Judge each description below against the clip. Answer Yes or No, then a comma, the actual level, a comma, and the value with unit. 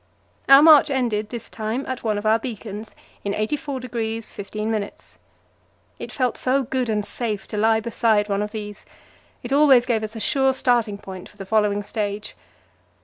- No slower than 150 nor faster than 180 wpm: Yes, average, 170 wpm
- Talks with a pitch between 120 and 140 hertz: No, high, 220 Hz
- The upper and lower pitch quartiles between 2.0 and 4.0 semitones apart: Yes, average, 3.3 semitones